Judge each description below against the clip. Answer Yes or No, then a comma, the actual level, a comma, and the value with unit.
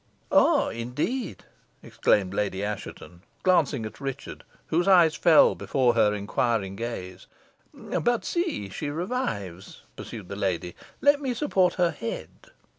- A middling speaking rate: No, slow, 125 wpm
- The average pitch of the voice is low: Yes, low, 125 Hz